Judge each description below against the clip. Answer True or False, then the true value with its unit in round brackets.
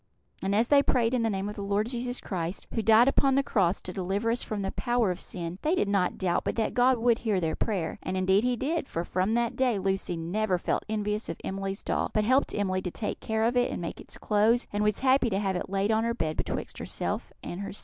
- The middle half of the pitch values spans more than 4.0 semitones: False (3.7 semitones)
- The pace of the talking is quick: True (260 wpm)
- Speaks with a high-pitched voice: True (210 Hz)